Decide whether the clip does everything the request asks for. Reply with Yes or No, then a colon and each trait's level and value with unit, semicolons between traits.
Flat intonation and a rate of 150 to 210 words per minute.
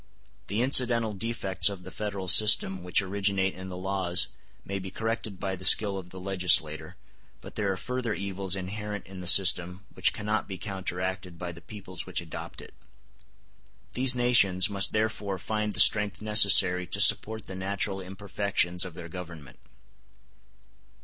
Yes: narrow, 2.3 semitones; average, 160 wpm